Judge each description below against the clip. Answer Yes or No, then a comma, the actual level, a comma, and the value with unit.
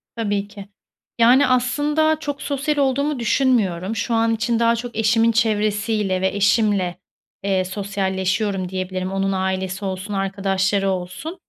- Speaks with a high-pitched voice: Yes, high, 205 Hz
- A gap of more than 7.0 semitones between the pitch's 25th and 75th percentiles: No, average, 3.7 semitones